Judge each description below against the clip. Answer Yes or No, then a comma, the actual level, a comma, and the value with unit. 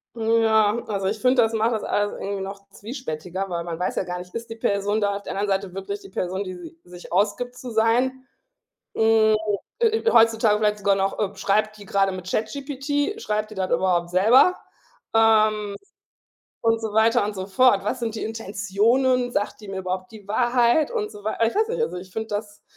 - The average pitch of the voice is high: Yes, high, 215 Hz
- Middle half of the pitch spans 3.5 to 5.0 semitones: No, average, 2.8 semitones